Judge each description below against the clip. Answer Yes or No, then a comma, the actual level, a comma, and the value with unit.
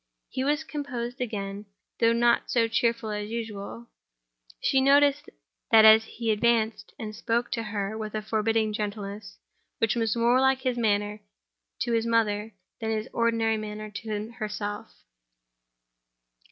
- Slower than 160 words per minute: Yes, average, 140 wpm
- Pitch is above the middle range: Yes, high, 225 Hz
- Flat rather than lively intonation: Yes, narrow, 1.9 semitones